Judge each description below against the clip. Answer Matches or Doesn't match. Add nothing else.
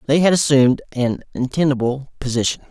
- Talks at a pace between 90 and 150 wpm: Matches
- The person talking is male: Matches